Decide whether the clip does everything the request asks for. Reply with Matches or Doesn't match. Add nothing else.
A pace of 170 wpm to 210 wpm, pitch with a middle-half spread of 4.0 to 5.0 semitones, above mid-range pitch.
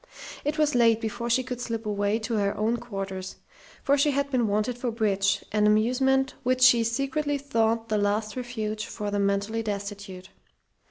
Doesn't match